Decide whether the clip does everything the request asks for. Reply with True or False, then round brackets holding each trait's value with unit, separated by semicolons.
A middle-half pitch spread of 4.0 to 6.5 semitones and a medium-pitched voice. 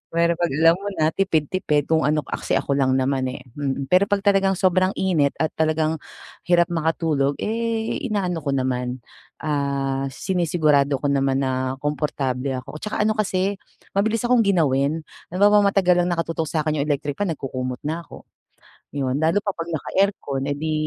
True (5.1 semitones; 155 Hz)